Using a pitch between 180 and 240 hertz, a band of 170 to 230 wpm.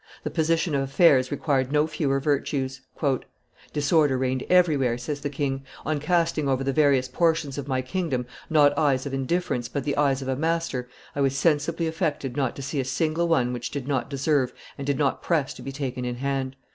No: medium, 140 Hz; average, 200 wpm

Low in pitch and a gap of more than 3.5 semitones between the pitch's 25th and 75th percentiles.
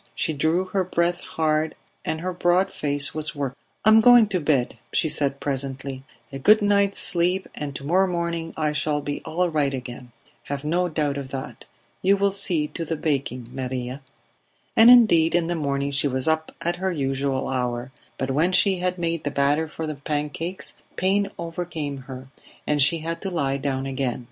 No: medium, 155 Hz; average, 4.2 semitones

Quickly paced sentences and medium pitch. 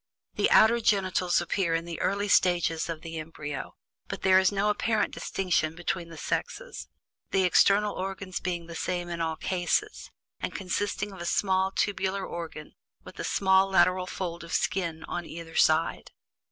No: average, 165 wpm; medium, 180 Hz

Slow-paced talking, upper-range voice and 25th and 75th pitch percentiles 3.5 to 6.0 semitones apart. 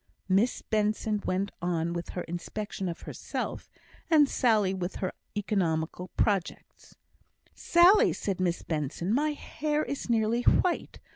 Yes: slow, 130 wpm; high, 200 Hz; average, 5.1 semitones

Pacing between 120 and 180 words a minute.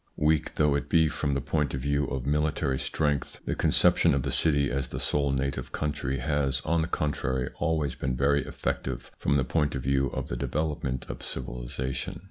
No: average, 200 wpm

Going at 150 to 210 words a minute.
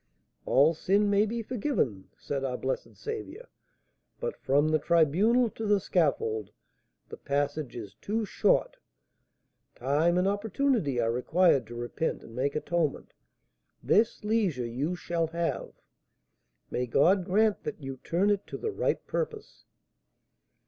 No: slow, 135 wpm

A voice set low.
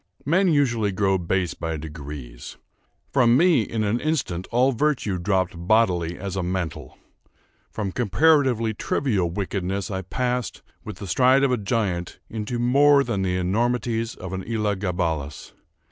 Yes: low, 105 Hz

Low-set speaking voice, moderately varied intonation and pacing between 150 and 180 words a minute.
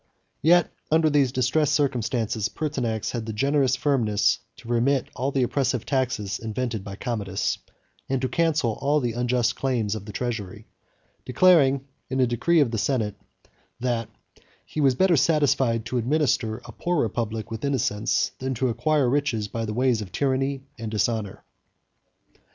Yes: low, 125 Hz; average, 3.8 semitones; average, 155 wpm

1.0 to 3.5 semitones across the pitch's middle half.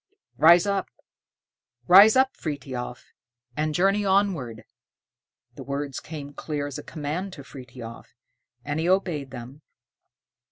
No: wide, 5.4 semitones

